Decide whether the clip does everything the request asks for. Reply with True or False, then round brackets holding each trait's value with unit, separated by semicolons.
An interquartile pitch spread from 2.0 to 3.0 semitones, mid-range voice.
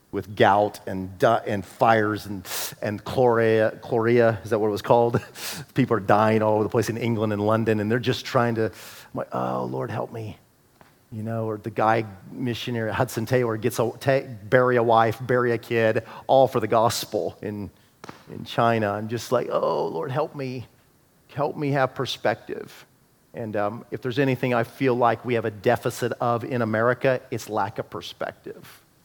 False (2.6 semitones; 115 Hz)